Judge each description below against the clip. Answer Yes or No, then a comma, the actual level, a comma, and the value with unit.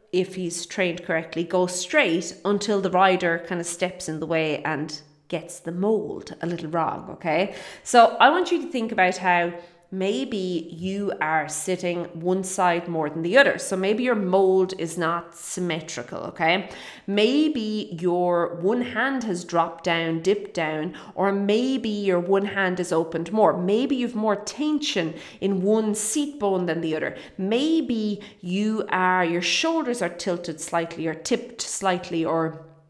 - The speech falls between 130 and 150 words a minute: No, average, 160 wpm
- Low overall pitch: No, medium, 185 Hz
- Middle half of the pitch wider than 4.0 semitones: No, average, 3.7 semitones